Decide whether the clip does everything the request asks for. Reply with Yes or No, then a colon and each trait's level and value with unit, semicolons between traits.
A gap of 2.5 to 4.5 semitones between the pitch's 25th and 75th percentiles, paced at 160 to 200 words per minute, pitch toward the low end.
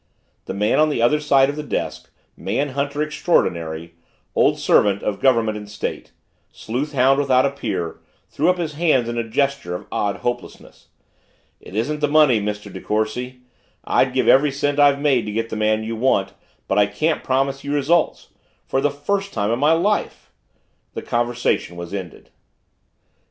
No: average, 5.3 semitones; average, 175 wpm; low, 130 Hz